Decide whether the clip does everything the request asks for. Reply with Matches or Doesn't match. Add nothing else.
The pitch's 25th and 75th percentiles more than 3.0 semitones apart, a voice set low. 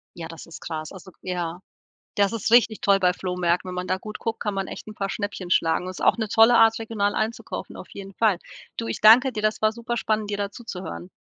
Doesn't match